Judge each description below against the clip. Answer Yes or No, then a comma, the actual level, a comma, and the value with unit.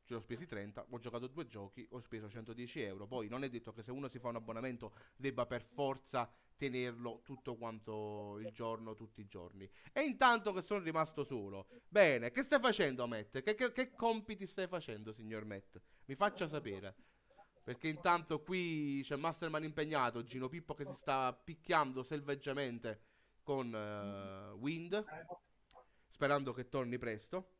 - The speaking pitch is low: Yes, low, 130 Hz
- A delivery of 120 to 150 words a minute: No, average, 165 wpm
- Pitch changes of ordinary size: No, wide, 5.8 semitones